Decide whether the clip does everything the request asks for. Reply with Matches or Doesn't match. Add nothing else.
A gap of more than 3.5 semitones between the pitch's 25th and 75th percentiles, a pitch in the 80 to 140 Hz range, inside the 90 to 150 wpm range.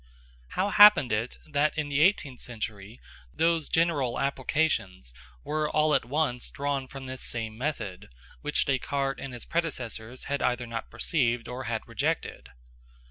Matches